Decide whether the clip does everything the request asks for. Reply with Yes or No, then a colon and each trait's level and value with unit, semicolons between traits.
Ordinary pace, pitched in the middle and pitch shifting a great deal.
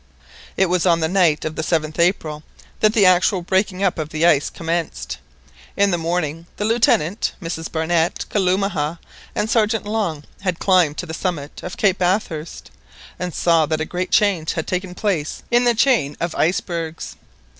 No: average, 175 wpm; medium, 175 Hz; average, 3.4 semitones